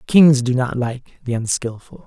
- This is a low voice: Yes, low, 130 Hz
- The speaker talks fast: No, average, 175 wpm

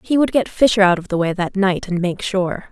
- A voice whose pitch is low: No, high, 195 Hz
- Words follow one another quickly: Yes, fast, 285 wpm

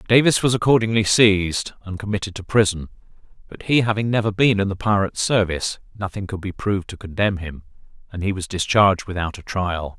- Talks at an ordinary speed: Yes, average, 185 wpm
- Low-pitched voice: Yes, low, 100 Hz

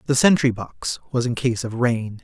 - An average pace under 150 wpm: No, fast, 215 wpm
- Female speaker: No, male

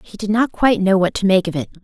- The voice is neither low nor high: No, high, 195 Hz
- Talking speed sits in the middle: No, fast, 330 wpm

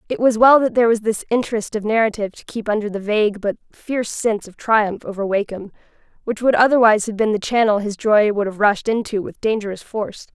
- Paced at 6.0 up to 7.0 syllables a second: Yes, 6.2 syllables/s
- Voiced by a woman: Yes, female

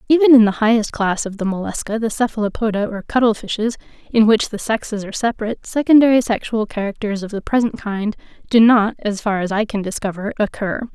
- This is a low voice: No, high, 215 Hz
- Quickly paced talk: No, average, 190 wpm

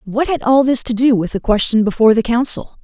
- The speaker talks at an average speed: No, fast, 255 wpm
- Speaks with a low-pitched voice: No, high, 235 Hz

